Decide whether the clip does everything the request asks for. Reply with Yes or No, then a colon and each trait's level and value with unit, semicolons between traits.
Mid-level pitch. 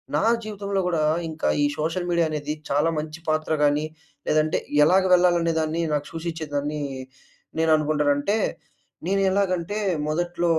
Yes: medium, 160 Hz